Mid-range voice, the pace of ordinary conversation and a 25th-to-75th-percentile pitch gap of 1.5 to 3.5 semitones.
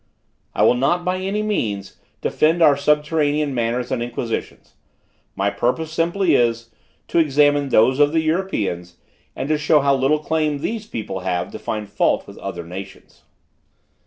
No: medium, 145 Hz; average, 155 wpm; wide, 5.5 semitones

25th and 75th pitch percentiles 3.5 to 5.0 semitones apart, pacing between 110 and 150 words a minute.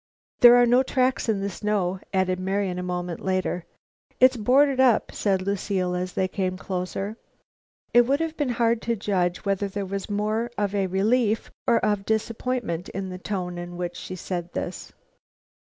No: average, 4.0 semitones; average, 170 wpm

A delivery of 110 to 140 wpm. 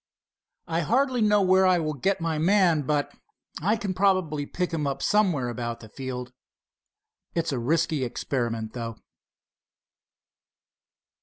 Yes: slow, 135 wpm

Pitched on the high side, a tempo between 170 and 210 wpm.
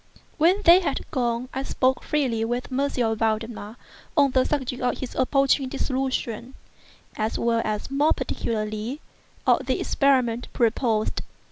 No: very high, 255 Hz; slow, 135 wpm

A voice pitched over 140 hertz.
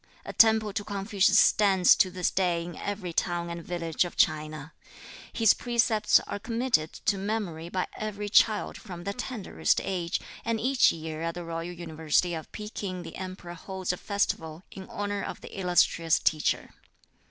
Yes: medium, 185 Hz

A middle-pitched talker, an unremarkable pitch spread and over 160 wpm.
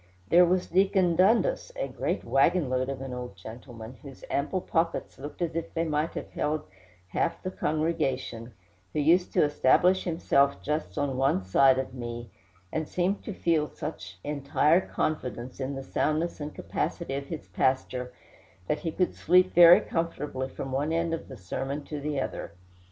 Yes: medium, 150 Hz; average, 4.2 semitones; average, 175 wpm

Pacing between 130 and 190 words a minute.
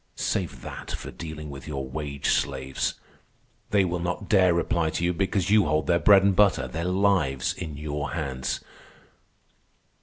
Yes: average, 160 wpm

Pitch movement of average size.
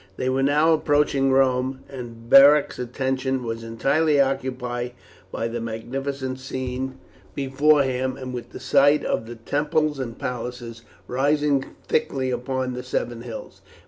No: narrow, 2.1 semitones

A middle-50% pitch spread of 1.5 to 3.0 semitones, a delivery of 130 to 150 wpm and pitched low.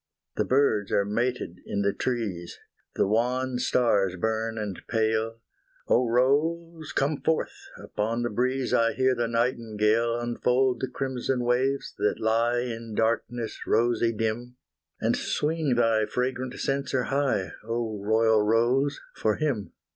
Yes: average, 2.7 semitones; slow, 135 wpm; low, 120 Hz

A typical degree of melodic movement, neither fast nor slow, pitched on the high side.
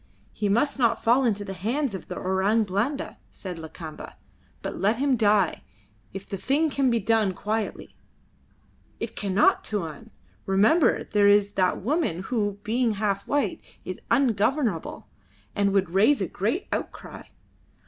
Yes: average, 3.9 semitones; average, 150 wpm; high, 210 Hz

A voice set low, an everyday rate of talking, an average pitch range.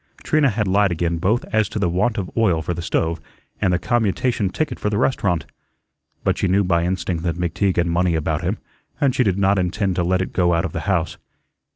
No: very low, 95 Hz; fast, 230 wpm; average, 3.3 semitones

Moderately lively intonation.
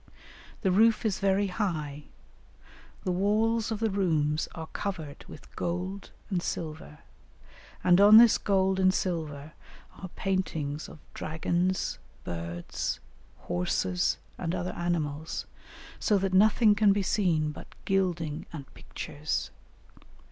Yes: average, 4.2 semitones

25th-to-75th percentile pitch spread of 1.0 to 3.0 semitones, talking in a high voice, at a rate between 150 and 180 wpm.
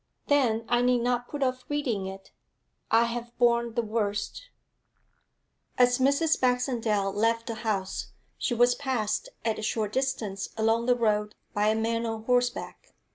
Yes: narrow, 2.4 semitones; high, 235 Hz; average, 155 wpm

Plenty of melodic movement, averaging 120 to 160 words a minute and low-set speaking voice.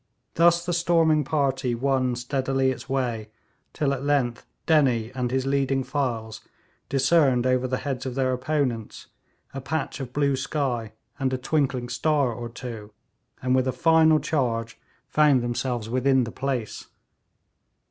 No: narrow, 2.6 semitones; average, 145 wpm; low, 130 Hz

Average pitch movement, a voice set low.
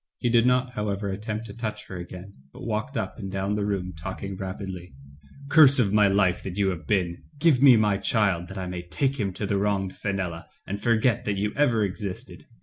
Yes: average, 3.1 semitones; low, 100 Hz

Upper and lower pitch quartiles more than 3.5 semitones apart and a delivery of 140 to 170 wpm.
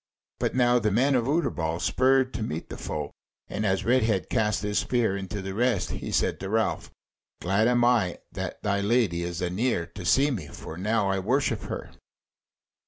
No: average, 4.5 semitones; average, 185 wpm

